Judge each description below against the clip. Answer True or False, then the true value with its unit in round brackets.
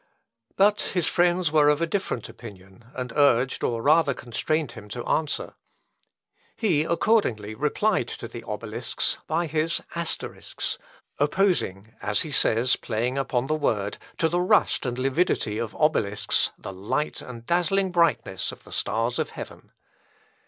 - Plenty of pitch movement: True (6.5 semitones)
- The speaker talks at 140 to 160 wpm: True (150 wpm)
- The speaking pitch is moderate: True (145 Hz)